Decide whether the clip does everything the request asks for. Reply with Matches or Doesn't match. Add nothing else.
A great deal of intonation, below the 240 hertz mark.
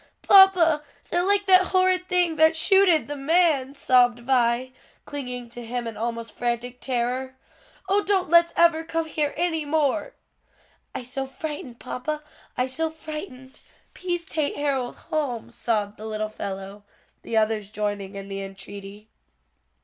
Doesn't match